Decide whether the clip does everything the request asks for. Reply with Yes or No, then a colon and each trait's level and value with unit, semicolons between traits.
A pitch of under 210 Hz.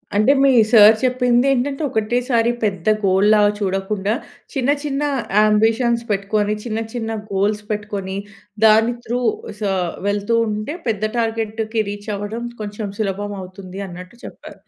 No: high, 215 Hz